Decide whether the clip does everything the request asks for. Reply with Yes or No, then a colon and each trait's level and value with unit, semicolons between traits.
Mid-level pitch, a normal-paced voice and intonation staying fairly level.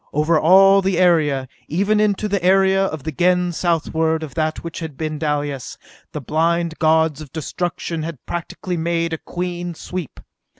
Yes: medium, 165 Hz; average, 170 wpm; narrow, 2.3 semitones